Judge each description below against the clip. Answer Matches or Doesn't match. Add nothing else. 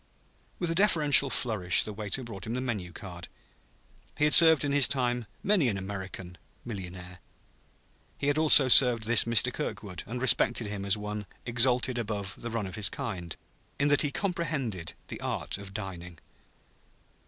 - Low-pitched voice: Matches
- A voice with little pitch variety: Doesn't match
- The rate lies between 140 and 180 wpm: Matches